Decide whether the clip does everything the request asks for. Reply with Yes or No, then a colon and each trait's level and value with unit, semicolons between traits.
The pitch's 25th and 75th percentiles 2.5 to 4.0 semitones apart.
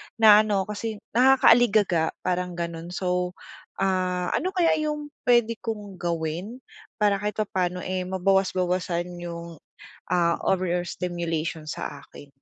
Yes: average, 3.6 semitones